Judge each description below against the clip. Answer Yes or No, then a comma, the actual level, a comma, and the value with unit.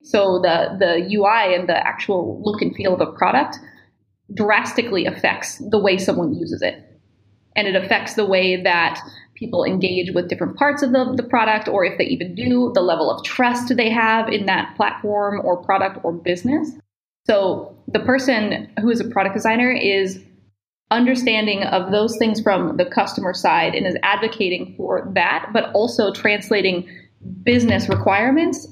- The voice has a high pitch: Yes, high, 210 Hz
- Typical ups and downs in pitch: Yes, average, 4.2 semitones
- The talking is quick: No, average, 165 wpm